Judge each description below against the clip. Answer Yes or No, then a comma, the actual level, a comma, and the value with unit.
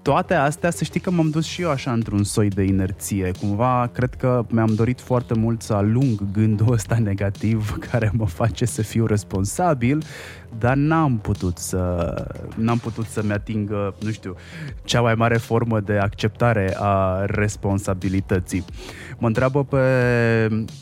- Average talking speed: Yes, average, 155 wpm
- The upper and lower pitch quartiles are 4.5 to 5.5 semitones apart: No, average, 3.6 semitones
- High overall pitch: No, low, 110 Hz